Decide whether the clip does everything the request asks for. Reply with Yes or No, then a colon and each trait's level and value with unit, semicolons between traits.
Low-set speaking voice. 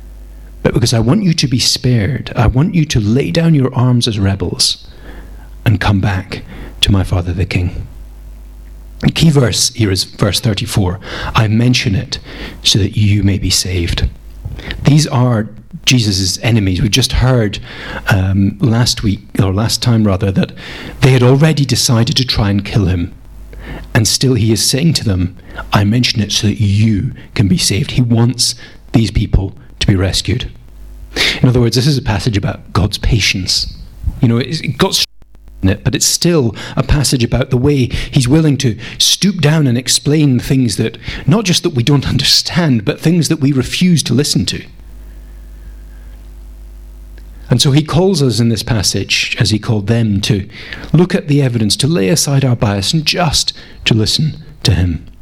Yes: low, 115 Hz